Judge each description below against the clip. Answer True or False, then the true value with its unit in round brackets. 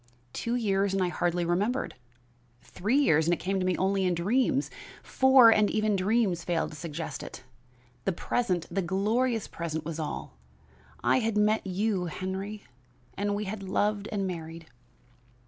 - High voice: True (195 Hz)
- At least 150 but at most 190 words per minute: True (165 wpm)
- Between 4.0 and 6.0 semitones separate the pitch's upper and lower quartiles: False (3.6 semitones)